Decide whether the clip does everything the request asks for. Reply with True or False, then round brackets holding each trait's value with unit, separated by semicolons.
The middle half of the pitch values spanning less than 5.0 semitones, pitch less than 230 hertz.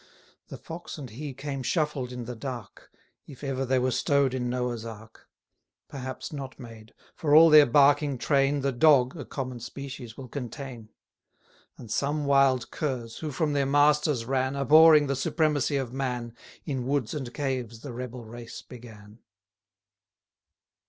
True (2.9 semitones; 135 Hz)